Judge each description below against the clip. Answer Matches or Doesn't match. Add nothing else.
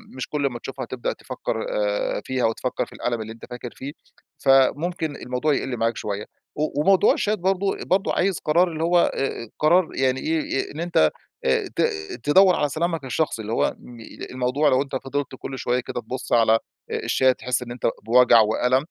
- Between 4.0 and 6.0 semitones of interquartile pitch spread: Matches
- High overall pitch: Doesn't match